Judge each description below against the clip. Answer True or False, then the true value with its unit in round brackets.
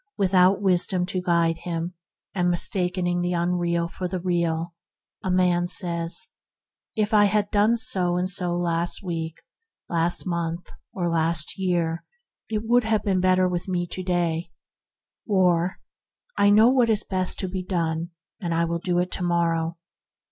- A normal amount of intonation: False (1.8 semitones)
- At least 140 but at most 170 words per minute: True (155 wpm)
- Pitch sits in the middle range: True (180 Hz)